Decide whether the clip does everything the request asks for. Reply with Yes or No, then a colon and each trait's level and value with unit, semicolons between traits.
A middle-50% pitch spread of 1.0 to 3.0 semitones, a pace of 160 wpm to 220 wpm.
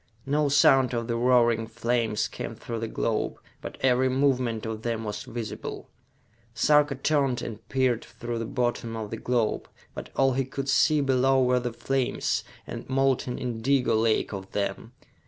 Yes: average, 2.7 semitones; average, 165 wpm